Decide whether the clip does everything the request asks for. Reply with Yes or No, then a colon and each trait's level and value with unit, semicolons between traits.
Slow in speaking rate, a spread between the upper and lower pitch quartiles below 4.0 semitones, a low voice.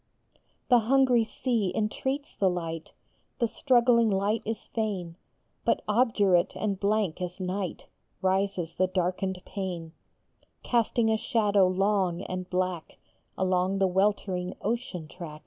No: slow, 125 wpm; average, 3.4 semitones; high, 195 Hz